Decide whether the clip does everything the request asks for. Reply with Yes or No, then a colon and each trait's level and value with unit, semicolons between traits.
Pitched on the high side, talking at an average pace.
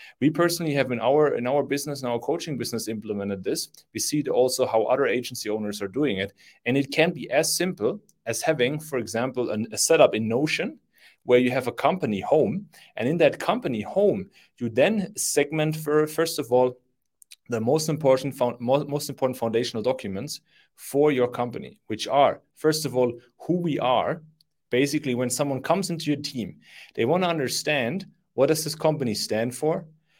No: medium, 140 Hz; average, 185 wpm